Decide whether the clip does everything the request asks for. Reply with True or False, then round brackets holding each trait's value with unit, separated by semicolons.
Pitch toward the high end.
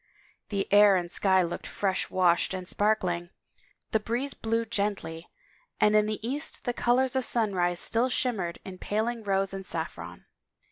True (205 Hz)